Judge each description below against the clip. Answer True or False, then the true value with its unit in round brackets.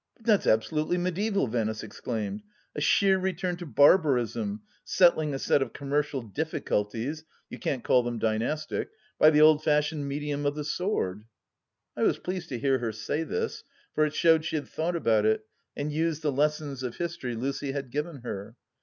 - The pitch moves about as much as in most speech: True (4.9 semitones)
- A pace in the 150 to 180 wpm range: False (200 wpm)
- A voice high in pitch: False (145 Hz)